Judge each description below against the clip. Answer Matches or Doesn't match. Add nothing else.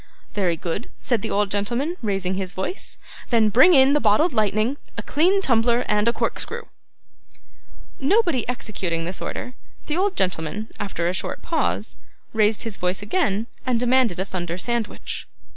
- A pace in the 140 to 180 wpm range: Matches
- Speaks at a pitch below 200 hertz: Doesn't match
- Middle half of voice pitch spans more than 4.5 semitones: Matches